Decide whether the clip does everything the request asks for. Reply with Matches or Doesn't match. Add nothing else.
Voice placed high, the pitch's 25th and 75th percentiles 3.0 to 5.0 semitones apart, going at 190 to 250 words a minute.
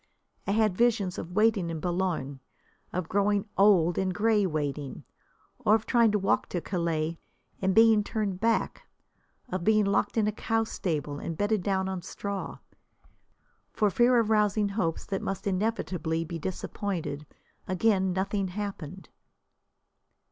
Doesn't match